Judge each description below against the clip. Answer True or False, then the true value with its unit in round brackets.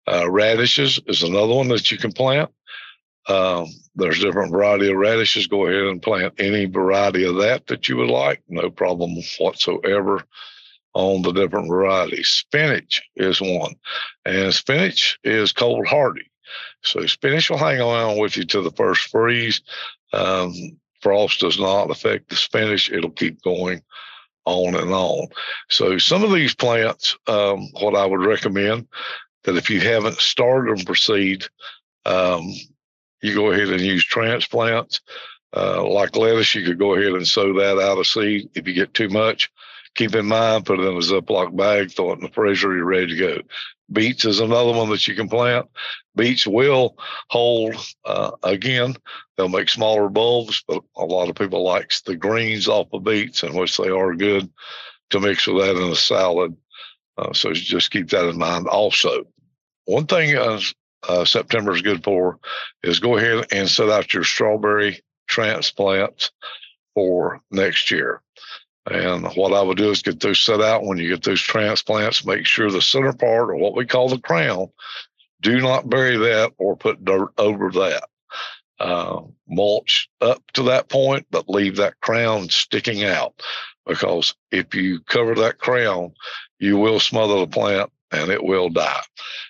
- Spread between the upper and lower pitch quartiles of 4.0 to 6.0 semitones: False (3.3 semitones)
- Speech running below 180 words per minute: True (170 wpm)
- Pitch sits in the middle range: False (100 Hz)